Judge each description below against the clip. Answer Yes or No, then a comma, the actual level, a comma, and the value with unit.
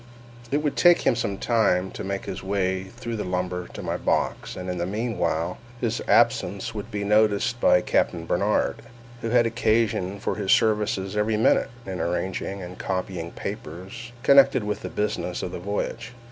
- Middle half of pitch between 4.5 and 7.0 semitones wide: No, average, 3.7 semitones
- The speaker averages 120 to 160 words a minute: No, average, 175 wpm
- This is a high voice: No, low, 100 Hz